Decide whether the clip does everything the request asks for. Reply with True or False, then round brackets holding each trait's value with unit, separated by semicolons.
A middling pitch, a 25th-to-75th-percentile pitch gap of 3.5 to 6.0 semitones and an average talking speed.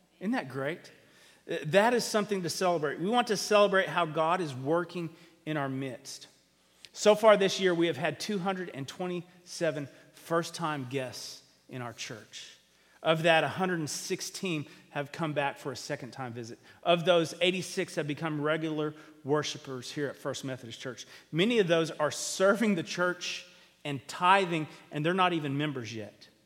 True (160 Hz; 3.9 semitones; 160 wpm)